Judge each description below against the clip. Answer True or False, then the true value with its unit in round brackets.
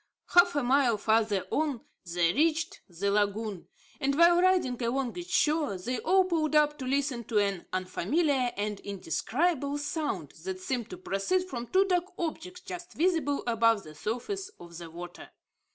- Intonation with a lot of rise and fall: True (8.3 semitones)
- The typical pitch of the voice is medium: False (275 Hz)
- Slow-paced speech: False (165 wpm)